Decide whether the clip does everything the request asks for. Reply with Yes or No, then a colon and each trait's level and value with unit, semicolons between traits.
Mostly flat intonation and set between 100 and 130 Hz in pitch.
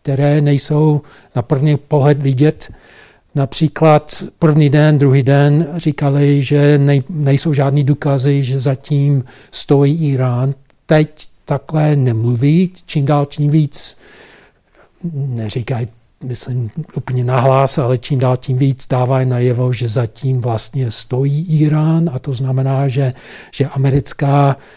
No: narrow, 2.2 semitones; medium, 140 Hz